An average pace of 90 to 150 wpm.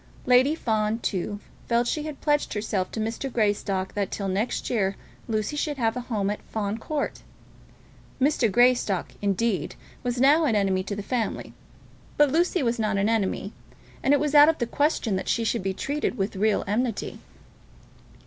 No: average, 180 wpm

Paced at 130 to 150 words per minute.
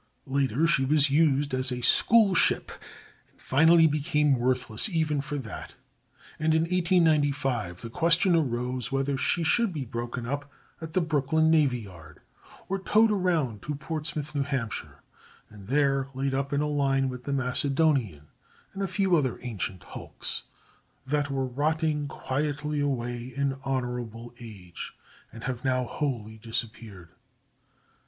Yes: average, 145 wpm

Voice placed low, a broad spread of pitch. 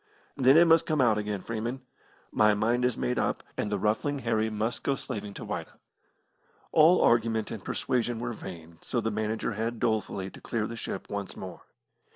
No: low, 115 Hz; average, 2.8 semitones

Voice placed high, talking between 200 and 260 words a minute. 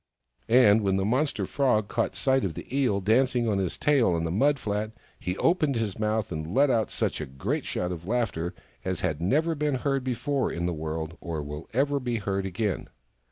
No: low, 110 Hz; fast, 205 wpm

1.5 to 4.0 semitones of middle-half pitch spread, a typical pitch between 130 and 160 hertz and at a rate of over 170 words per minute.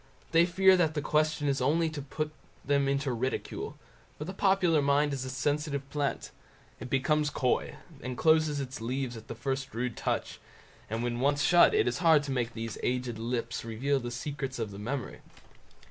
Yes: average, 3.4 semitones; medium, 140 Hz; average, 190 wpm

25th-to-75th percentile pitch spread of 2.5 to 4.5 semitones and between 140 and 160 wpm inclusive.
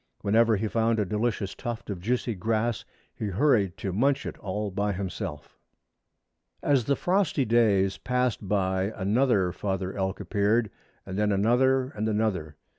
Yes: average, 3.5 semitones; average, 150 wpm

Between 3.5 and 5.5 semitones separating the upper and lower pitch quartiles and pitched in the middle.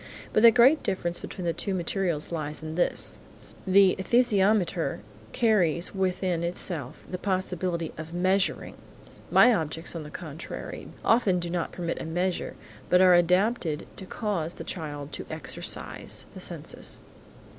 No: average, 2.7 semitones; medium, 180 Hz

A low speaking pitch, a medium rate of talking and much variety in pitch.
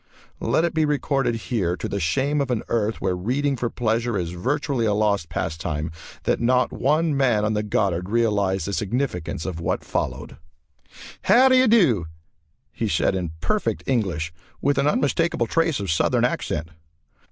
Yes: low, 115 Hz; average, 170 wpm; wide, 7.0 semitones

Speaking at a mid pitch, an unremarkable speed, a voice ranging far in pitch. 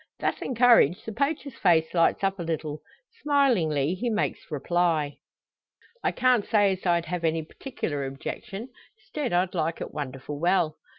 Yes: medium, 175 Hz; average, 155 wpm; wide, 6.0 semitones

